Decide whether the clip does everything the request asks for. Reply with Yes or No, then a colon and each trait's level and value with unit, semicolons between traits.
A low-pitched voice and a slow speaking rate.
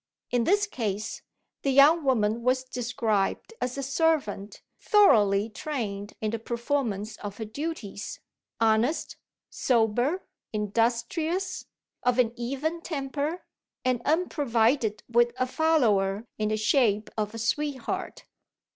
No: high, 240 Hz; slow, 120 wpm